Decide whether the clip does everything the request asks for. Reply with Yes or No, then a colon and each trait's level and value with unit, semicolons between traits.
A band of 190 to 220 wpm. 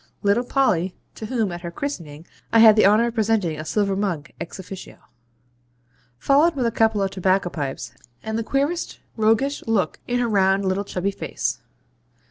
No: average, 175 wpm